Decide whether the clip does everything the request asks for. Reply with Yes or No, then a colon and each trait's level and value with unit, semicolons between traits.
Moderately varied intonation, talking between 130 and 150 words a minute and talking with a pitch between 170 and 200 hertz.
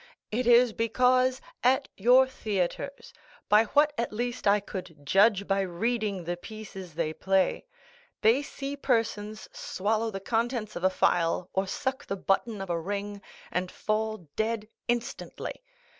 No: average, 3.8 semitones; average, 145 wpm; high, 215 Hz